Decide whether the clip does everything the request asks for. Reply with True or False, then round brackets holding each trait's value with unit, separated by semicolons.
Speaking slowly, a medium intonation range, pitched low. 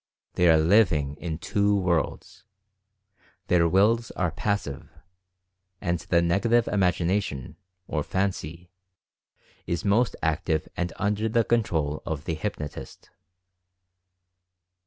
True (110 wpm; 4.0 semitones; 90 Hz)